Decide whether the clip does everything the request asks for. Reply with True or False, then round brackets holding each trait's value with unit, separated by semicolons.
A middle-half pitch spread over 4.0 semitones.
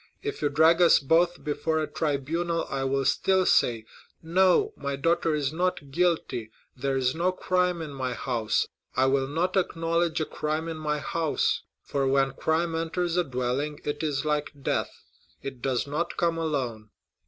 False (3.7 semitones)